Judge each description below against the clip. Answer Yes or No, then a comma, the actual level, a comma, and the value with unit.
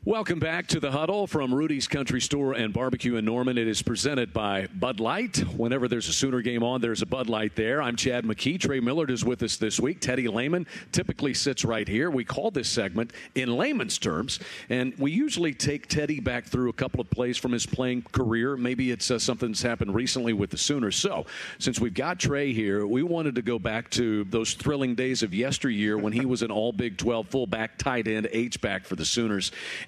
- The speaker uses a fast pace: Yes, fast, 220 wpm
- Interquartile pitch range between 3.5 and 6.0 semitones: No, average, 2.9 semitones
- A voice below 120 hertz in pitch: No, low, 125 Hz